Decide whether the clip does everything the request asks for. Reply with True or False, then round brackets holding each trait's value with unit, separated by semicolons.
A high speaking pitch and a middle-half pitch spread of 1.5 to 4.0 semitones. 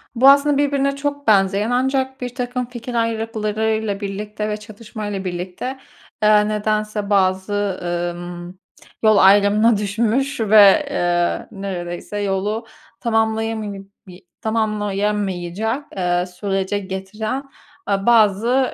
True (210 Hz; 2.9 semitones)